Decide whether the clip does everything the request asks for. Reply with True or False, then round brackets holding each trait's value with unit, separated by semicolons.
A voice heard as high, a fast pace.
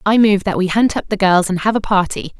True (200 Hz; 300 wpm)